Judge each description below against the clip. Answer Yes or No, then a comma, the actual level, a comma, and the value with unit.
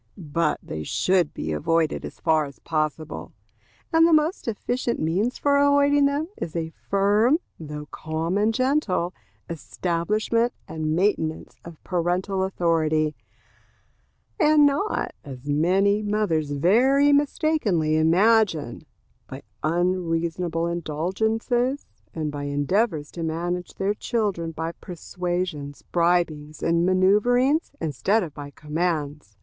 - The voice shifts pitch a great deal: Yes, wide, 5.7 semitones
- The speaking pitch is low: No, medium, 175 Hz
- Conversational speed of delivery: No, slow, 115 wpm